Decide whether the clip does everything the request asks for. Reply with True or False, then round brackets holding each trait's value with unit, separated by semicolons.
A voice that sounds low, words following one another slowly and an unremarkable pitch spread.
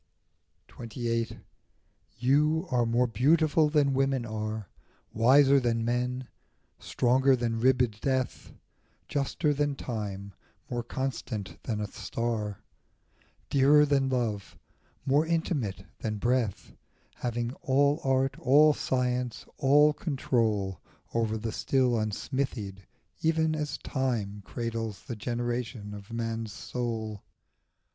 True (120 Hz; 110 wpm; 3.5 semitones)